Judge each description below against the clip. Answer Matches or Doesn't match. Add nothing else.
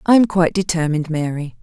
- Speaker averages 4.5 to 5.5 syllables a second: Doesn't match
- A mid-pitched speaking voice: Matches